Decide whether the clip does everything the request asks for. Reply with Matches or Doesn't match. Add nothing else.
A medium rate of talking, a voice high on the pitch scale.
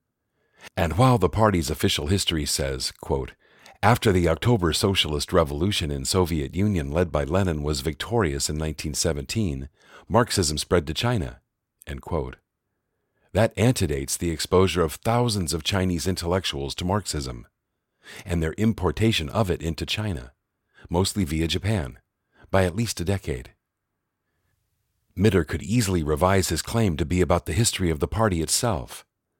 Doesn't match